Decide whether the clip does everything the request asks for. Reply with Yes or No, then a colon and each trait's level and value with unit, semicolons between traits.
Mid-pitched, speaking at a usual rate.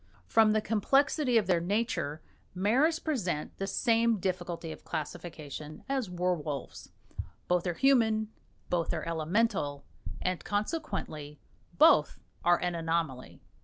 No: medium, 180 Hz; slow, 120 wpm